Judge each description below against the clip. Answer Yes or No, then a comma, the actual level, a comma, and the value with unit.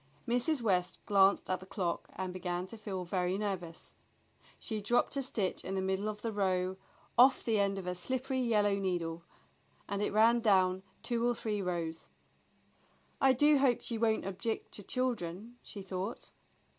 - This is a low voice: No, high, 200 Hz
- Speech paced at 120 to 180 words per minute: Yes, average, 170 wpm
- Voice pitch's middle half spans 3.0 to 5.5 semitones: Yes, average, 4.0 semitones